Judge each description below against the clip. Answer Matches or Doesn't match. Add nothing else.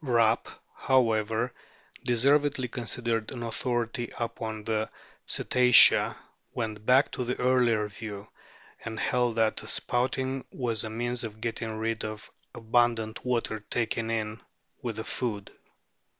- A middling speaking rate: Doesn't match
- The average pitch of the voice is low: Matches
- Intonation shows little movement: Matches